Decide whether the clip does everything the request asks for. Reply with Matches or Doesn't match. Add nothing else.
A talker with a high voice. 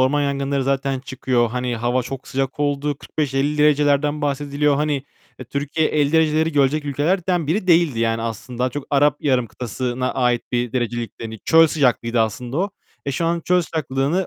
Doesn't match